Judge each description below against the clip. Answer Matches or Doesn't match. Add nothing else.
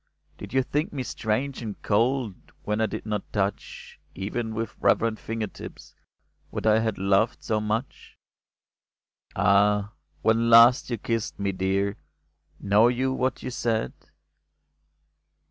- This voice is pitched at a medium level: Doesn't match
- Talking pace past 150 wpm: Doesn't match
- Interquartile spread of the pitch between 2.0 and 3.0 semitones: Matches